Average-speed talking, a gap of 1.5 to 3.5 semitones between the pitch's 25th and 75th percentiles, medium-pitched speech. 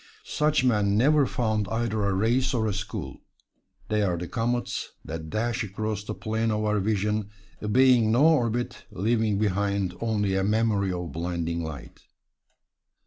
No: average, 150 wpm; average, 2.9 semitones; low, 105 Hz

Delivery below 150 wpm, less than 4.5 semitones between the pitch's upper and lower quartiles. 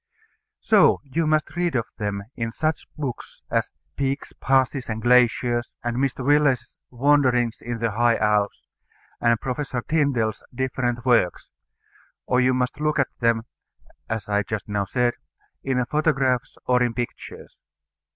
Yes: average, 140 wpm; average, 2.9 semitones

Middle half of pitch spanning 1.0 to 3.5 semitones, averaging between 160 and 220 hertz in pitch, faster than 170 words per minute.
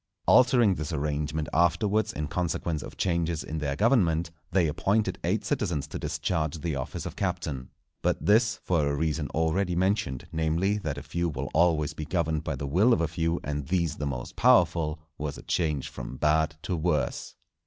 No: average, 2.8 semitones; very low, 80 Hz; average, 185 wpm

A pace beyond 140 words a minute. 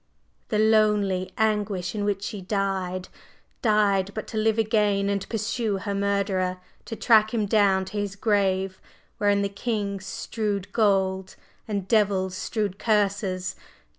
No: slow, 135 wpm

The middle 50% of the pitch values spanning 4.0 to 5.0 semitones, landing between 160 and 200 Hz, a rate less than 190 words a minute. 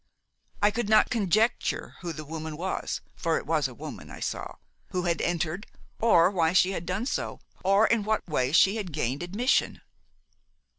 Yes: average, 4.4 semitones; medium, 185 Hz; average, 180 wpm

